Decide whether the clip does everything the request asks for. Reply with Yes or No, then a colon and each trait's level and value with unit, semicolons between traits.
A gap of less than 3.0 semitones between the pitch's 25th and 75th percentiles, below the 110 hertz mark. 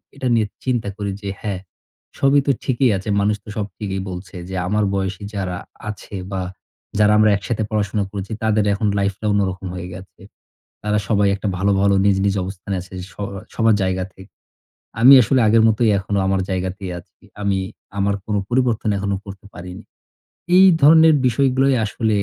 Yes: narrow, 2.4 semitones; low, 100 Hz